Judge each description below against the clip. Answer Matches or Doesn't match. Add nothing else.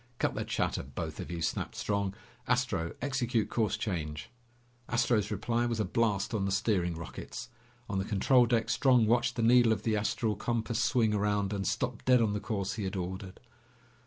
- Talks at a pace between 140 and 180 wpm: Doesn't match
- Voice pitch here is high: Doesn't match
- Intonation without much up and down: Doesn't match